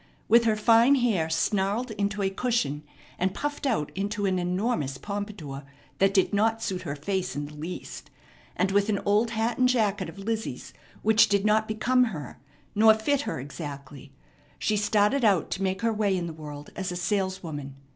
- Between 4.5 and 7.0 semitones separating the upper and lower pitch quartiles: No, average, 3.9 semitones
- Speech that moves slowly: No, average, 185 wpm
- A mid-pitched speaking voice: No, high, 200 Hz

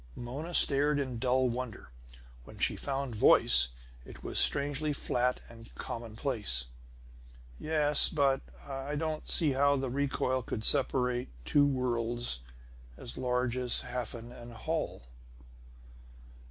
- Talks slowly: Yes, slow, 120 wpm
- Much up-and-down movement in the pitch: No, average, 2.9 semitones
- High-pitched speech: No, low, 130 Hz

